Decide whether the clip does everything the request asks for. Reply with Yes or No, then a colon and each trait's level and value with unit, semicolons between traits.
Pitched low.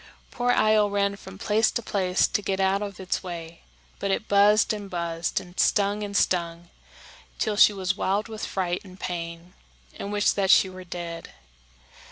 No: high, 195 Hz